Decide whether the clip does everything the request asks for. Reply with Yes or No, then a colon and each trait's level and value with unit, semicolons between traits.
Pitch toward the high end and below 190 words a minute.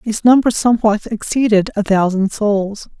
Yes: high, 215 Hz; average, 140 wpm